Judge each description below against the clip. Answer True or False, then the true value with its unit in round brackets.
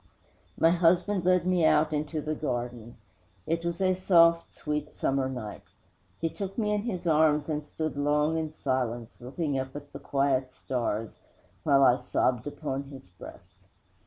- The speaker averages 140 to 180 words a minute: True (160 wpm)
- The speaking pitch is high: False (150 Hz)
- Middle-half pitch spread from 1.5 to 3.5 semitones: False (4.1 semitones)